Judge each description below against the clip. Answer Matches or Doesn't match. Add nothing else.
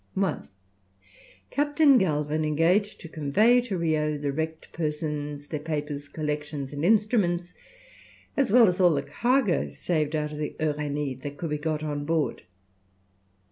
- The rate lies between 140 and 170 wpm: Matches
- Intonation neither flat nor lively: Matches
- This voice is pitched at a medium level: Matches